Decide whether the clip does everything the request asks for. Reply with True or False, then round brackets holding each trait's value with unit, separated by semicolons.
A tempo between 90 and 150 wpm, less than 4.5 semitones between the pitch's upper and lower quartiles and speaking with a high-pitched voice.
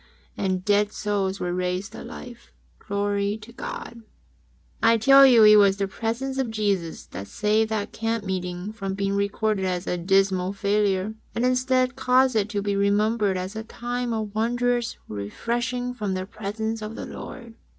False (170 wpm; 3.0 semitones; 210 Hz)